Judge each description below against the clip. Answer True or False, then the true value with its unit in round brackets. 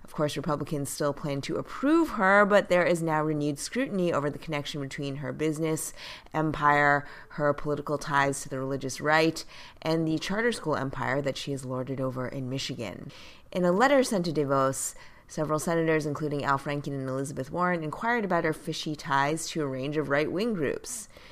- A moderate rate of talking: True (185 wpm)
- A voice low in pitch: False (150 Hz)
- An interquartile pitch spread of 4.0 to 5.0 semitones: False (2.8 semitones)